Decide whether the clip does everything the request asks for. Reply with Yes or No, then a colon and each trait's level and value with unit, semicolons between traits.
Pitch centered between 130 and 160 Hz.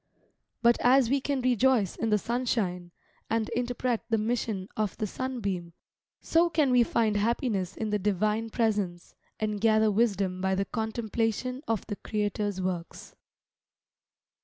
No: high, 220 Hz